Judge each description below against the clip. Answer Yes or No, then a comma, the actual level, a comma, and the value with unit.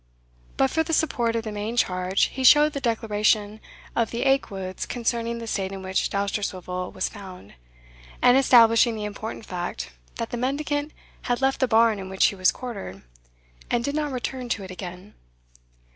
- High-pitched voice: Yes, high, 225 Hz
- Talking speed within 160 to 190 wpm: Yes, average, 175 wpm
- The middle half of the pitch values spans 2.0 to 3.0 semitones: No, average, 4.5 semitones